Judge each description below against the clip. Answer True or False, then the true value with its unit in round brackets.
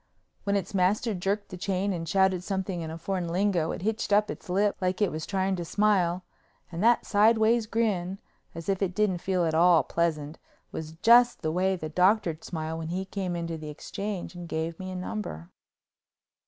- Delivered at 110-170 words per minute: False (195 wpm)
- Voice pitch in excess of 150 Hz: True (185 Hz)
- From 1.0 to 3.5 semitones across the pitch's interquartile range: True (3.2 semitones)